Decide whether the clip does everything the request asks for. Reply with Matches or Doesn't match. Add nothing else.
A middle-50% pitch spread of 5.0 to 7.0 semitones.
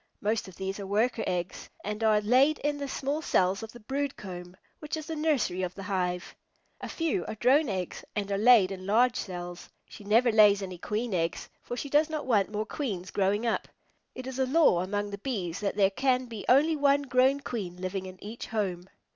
Matches